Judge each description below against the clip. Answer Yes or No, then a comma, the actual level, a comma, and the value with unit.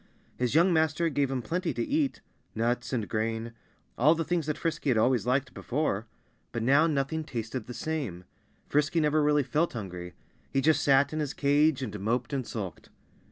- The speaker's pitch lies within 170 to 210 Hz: No, low, 135 Hz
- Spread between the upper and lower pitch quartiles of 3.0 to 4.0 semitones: No, average, 5.1 semitones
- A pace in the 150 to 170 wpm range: No, average, 185 wpm